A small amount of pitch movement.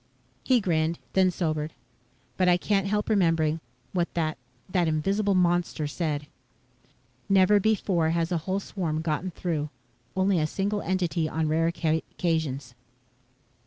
No: average, 3.2 semitones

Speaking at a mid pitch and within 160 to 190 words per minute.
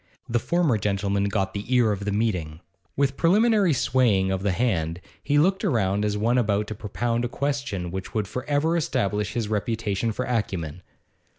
No: low, 110 Hz; average, 180 wpm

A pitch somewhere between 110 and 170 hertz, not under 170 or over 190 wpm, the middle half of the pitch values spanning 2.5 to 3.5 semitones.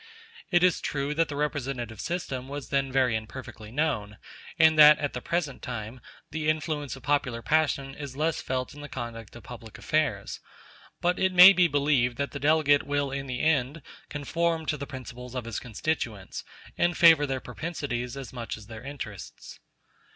No: medium, 140 Hz; average, 180 wpm; average, 3.9 semitones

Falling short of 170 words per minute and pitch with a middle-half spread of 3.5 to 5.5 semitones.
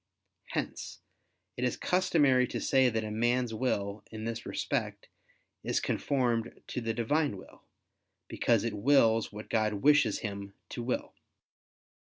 No: average, 140 wpm; average, 3.0 semitones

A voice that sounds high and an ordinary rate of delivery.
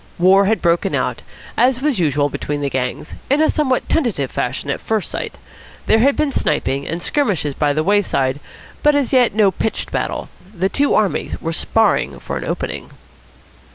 Yes: high, 195 Hz; average, 180 wpm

